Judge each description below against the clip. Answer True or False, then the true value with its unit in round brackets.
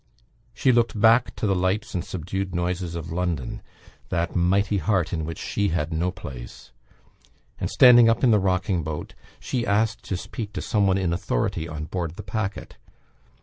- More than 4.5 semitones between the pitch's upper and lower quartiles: False (3.7 semitones)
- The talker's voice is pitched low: True (95 Hz)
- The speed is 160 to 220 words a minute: True (180 wpm)